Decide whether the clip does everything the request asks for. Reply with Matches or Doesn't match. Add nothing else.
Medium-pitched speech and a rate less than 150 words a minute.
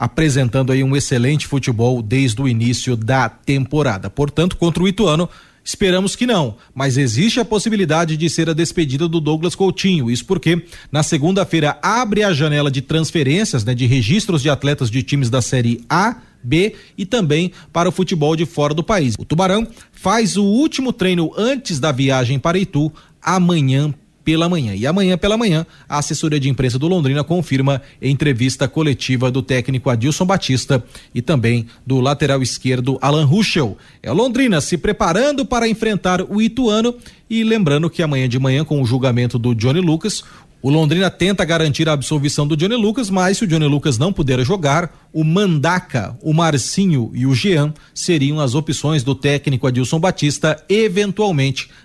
Doesn't match